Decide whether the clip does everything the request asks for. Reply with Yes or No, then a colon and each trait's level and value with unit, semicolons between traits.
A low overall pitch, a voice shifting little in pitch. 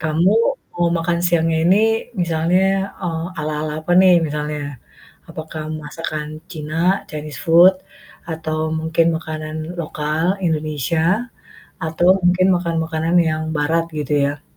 No: medium, 160 Hz; narrow, 1.9 semitones